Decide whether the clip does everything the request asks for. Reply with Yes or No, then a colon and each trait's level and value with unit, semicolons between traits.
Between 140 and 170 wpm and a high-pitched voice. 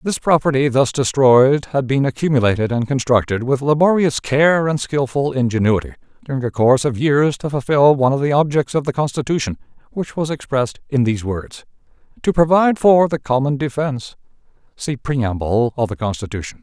No: average, 165 wpm; low, 135 Hz